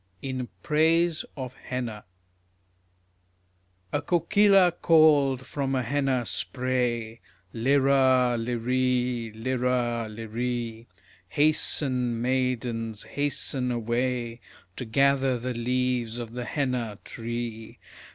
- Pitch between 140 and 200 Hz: No, low, 125 Hz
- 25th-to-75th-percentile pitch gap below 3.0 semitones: Yes, narrow, 2.4 semitones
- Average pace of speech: No, slow, 90 wpm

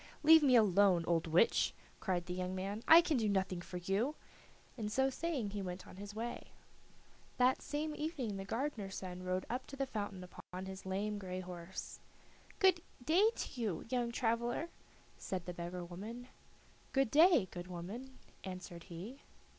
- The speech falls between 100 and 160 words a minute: No, average, 170 wpm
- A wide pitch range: Yes, wide, 5.9 semitones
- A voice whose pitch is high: Yes, high, 205 Hz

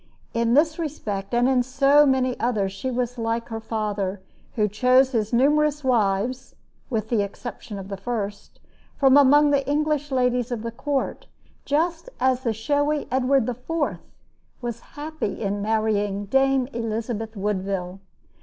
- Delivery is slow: No, average, 145 wpm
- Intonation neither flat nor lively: Yes, average, 4.2 semitones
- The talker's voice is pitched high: Yes, high, 245 Hz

